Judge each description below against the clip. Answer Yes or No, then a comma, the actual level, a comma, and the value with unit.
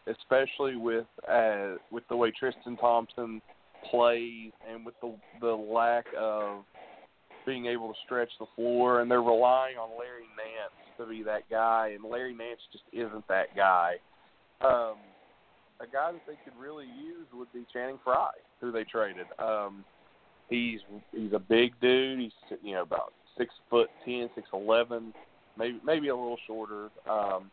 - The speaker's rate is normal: Yes, average, 160 wpm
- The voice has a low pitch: Yes, low, 115 Hz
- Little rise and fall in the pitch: Yes, narrow, 1.7 semitones